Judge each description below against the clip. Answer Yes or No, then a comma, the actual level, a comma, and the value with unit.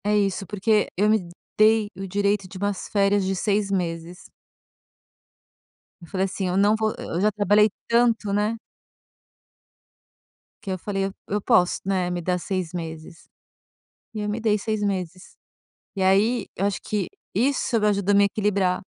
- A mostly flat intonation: Yes, narrow, 2.1 semitones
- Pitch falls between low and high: No, high, 200 Hz